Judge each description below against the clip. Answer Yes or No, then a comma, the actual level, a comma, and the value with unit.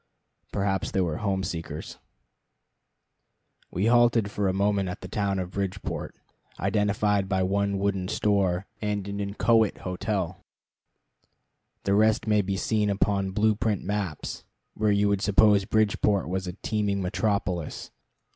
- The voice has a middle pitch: No, low, 100 Hz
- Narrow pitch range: Yes, narrow, 1.6 semitones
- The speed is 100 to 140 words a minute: Yes, slow, 135 wpm